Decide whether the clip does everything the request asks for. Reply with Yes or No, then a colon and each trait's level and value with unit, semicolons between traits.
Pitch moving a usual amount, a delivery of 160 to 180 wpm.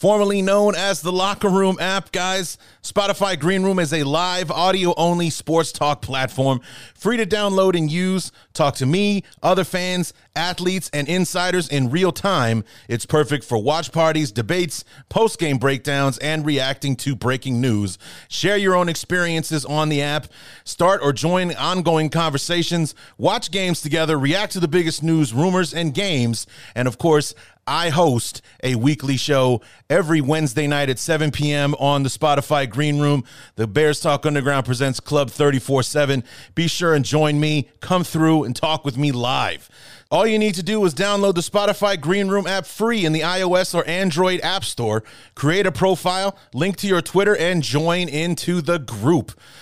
Yes: average, 4.6 semitones; average, 170 wpm